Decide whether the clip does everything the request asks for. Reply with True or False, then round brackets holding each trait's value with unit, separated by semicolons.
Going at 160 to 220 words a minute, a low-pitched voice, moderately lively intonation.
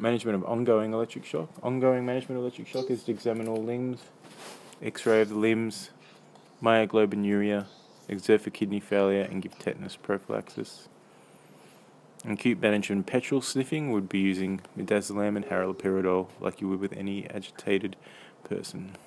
False (145 wpm; 105 Hz; 3.0 semitones)